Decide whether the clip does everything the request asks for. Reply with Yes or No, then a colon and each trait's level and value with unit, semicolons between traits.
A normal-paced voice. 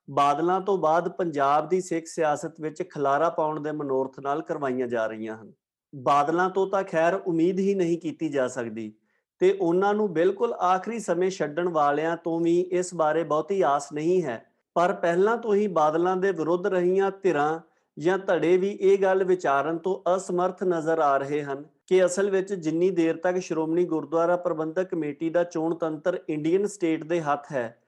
No: fast, 175 wpm